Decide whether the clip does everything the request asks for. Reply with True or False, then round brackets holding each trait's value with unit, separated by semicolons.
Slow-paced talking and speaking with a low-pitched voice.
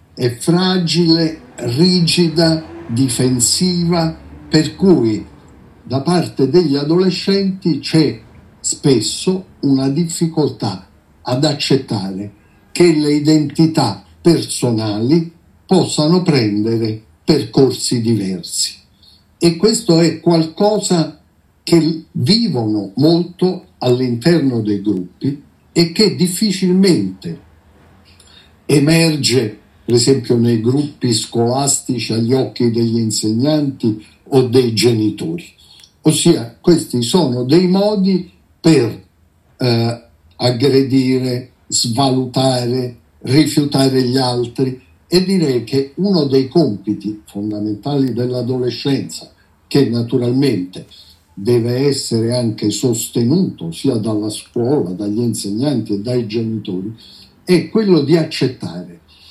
True (90 wpm; 130 Hz)